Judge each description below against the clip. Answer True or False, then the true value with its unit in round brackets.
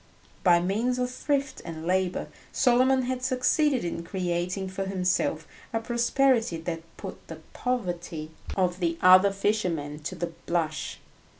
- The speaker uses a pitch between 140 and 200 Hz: True (185 Hz)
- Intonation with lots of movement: True (6.4 semitones)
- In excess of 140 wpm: False (135 wpm)